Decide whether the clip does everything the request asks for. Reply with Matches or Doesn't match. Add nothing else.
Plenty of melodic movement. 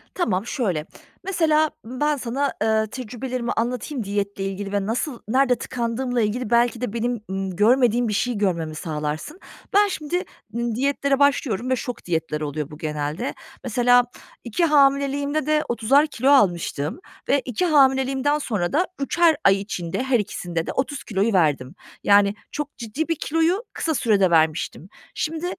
Matches